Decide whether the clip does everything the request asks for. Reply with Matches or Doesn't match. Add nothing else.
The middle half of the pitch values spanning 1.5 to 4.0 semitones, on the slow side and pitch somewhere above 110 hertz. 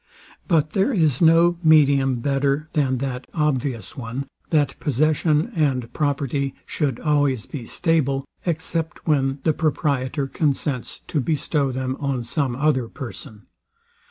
Matches